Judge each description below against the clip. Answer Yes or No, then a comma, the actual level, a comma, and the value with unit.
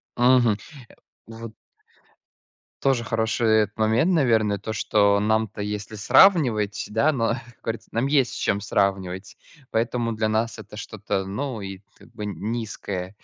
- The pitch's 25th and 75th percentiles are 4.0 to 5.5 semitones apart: No, narrow, 2.6 semitones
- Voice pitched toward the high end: No, low, 110 Hz